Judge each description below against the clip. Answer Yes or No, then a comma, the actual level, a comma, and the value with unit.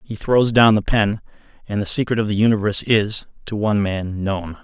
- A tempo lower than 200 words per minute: No, fast, 205 wpm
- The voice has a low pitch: Yes, low, 105 Hz